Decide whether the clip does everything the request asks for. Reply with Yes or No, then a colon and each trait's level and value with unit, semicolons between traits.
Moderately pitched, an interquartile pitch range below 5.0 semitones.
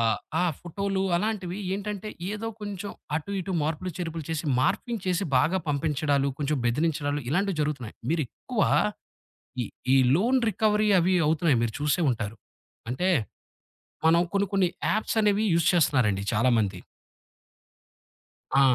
No: medium, 165 Hz; wide, 5.6 semitones